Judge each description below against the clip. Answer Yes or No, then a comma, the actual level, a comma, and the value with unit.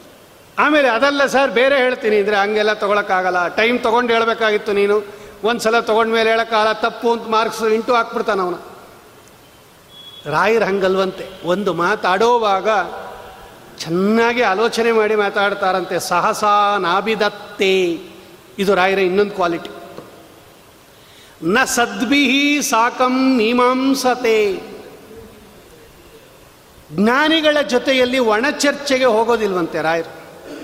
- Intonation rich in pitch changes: No, average, 3.6 semitones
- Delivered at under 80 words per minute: No, average, 85 wpm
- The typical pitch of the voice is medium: No, high, 220 Hz